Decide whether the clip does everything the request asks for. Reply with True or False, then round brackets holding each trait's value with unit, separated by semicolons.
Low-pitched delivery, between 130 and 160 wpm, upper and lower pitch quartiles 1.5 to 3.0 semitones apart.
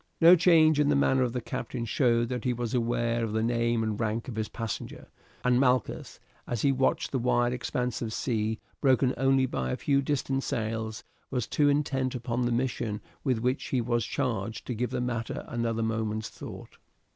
False (120 Hz; 195 wpm; 2.4 semitones)